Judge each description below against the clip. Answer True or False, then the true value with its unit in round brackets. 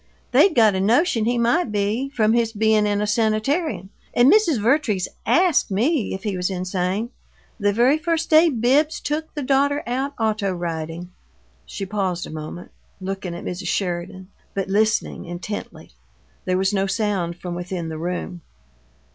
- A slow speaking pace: False (165 wpm)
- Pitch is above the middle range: True (210 Hz)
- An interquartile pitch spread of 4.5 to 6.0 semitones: True (5.6 semitones)